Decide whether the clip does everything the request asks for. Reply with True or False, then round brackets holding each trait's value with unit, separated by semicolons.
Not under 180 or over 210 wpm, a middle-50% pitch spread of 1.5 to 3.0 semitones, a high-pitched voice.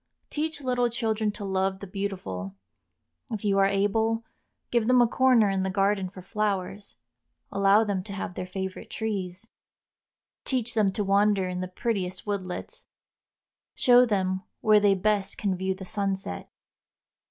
False (155 wpm; 2.6 semitones; 200 Hz)